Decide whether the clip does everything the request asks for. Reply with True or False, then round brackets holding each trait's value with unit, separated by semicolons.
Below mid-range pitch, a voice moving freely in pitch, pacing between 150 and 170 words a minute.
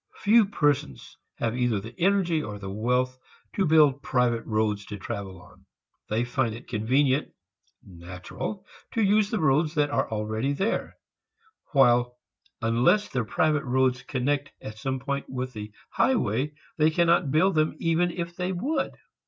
True (130 Hz; 6.1 semitones; 155 wpm)